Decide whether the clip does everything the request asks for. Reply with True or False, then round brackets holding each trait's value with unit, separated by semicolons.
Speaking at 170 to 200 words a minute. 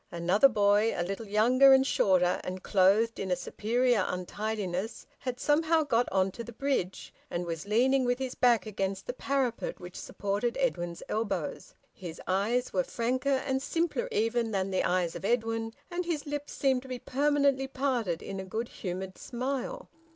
True (175 wpm)